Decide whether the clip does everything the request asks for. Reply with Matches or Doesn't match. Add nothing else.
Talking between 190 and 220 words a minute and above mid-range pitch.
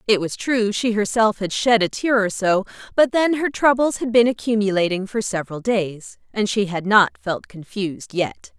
Matches